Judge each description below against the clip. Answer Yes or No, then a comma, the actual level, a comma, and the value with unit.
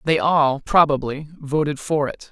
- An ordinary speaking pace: Yes, average, 155 wpm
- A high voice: No, medium, 145 Hz